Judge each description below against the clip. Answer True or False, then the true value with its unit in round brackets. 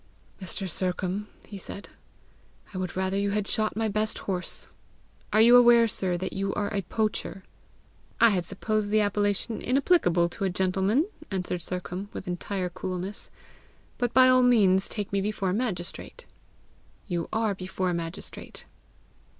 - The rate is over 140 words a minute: True (155 wpm)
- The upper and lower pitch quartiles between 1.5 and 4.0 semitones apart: True (2.7 semitones)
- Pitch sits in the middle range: False (195 Hz)